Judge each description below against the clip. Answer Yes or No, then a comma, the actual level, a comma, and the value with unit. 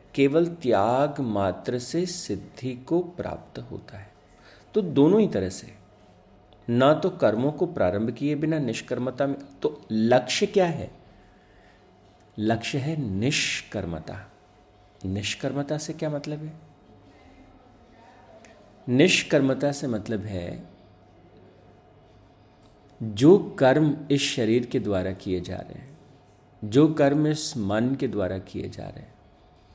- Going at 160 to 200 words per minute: No, average, 120 wpm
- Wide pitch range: Yes, wide, 5.9 semitones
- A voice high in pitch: No, low, 120 Hz